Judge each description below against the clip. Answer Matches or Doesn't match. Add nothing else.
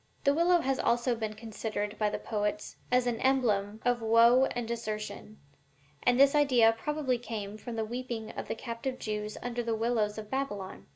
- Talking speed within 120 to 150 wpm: Doesn't match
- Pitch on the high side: Matches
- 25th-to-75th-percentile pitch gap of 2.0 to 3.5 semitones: Matches